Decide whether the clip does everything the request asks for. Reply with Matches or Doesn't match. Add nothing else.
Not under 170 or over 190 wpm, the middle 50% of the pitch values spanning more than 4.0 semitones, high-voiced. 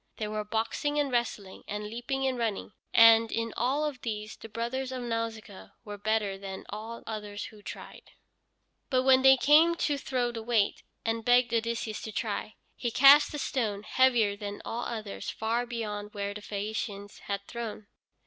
Doesn't match